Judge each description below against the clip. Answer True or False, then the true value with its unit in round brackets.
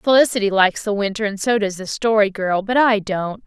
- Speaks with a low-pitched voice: False (210 Hz)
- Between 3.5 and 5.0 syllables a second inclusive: False (5.5 syllables/s)